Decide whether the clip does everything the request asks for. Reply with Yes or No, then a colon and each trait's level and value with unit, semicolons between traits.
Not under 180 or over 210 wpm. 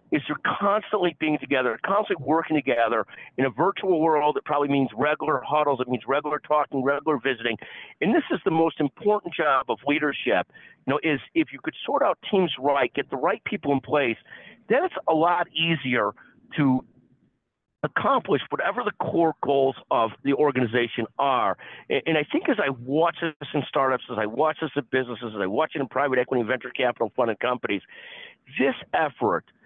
Yes: average, 185 wpm